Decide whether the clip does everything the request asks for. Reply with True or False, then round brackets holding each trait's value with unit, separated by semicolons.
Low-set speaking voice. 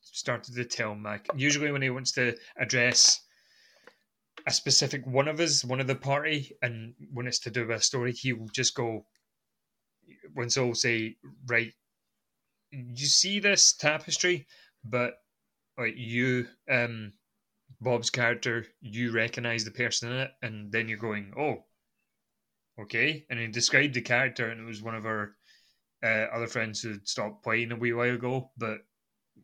True (120 Hz)